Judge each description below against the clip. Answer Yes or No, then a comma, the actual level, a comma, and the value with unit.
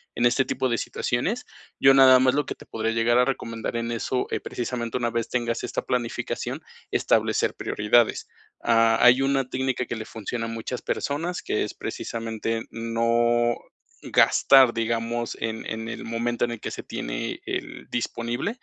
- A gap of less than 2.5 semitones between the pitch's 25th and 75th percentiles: Yes, narrow, 1.7 semitones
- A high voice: No, low, 120 Hz